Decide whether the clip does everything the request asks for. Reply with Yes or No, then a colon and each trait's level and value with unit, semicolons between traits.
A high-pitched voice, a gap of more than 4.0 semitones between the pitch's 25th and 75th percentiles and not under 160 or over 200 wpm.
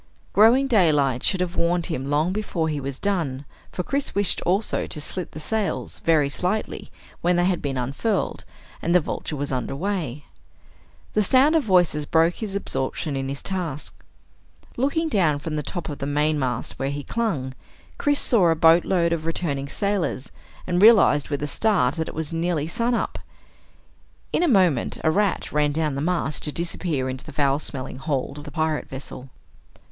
No: medium, 160 Hz; average, 5.0 semitones; average, 180 wpm